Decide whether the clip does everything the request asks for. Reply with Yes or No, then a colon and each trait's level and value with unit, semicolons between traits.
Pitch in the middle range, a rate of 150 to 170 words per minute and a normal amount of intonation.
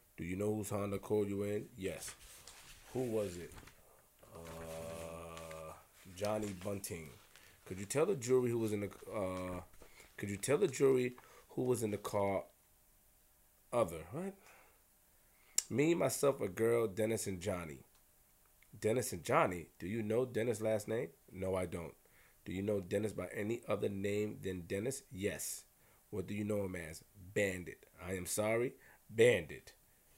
No: low, 100 Hz; average, 155 wpm; average, 3.5 semitones